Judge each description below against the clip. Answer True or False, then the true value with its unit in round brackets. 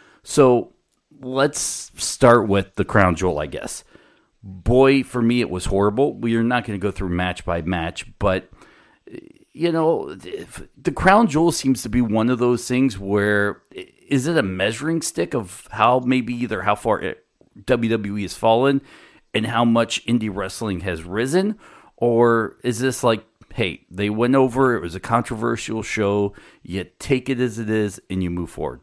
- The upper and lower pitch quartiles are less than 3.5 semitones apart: False (4.6 semitones)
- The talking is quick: False (175 wpm)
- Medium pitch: False (115 Hz)